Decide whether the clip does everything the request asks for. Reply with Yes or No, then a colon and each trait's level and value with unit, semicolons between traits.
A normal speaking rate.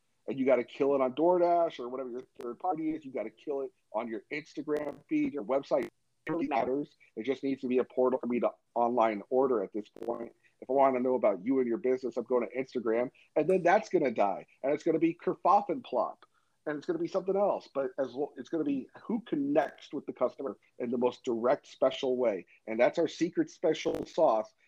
No: fast, 245 wpm